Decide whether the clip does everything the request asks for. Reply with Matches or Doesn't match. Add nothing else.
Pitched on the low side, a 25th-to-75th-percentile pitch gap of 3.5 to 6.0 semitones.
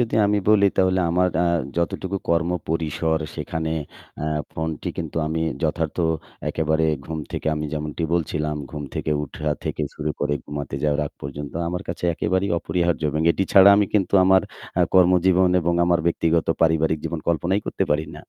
Doesn't match